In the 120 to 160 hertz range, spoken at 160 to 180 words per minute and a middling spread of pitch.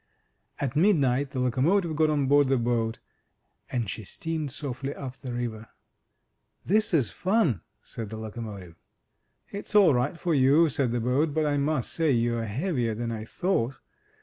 Yes: low, 135 Hz; average, 165 wpm; average, 4.9 semitones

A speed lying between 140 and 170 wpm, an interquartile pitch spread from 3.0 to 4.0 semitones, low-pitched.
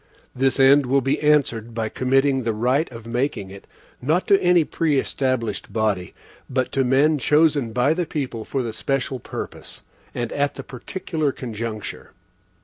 Yes: average, 155 wpm; average, 3.7 semitones; low, 130 Hz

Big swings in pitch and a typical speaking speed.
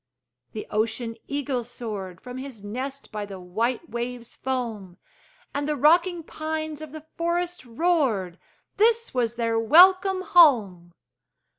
No: wide, 6.1 semitones; slow, 130 wpm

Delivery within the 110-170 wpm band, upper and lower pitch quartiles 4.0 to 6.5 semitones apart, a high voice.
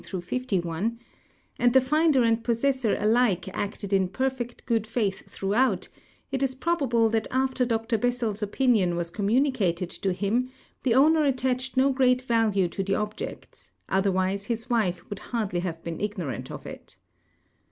Yes: average, 160 wpm; average, 4.6 semitones; high, 225 Hz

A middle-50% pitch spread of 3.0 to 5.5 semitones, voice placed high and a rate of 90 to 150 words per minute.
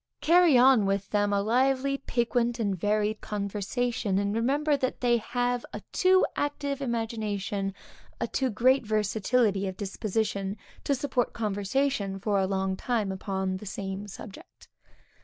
Yes: average, 4.0 semitones; high, 215 Hz; average, 140 wpm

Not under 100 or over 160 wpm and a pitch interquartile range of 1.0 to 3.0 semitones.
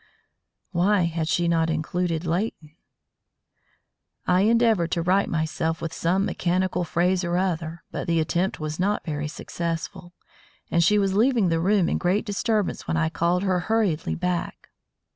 Yes: average, 155 wpm; narrow, 2.6 semitones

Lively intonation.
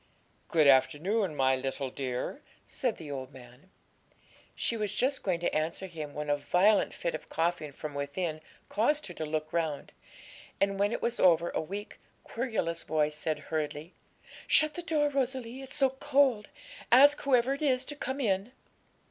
Yes: wide, 8.9 semitones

